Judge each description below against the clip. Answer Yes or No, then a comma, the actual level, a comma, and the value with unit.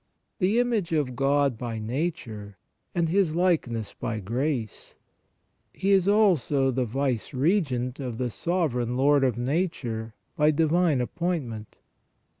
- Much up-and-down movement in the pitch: Yes, wide, 6.0 semitones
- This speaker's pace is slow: Yes, slow, 125 wpm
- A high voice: No, medium, 140 Hz